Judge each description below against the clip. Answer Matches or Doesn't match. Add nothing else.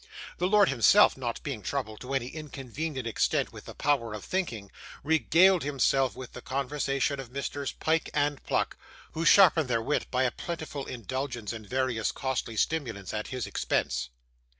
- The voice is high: Doesn't match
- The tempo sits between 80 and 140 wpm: Doesn't match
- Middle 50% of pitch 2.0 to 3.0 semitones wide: Doesn't match